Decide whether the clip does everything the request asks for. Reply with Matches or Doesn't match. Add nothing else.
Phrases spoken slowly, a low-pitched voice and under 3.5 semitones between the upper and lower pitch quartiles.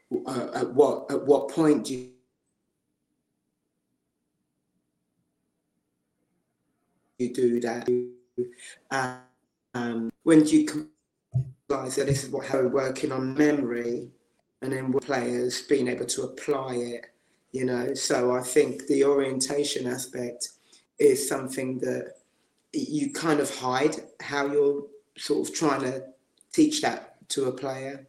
Matches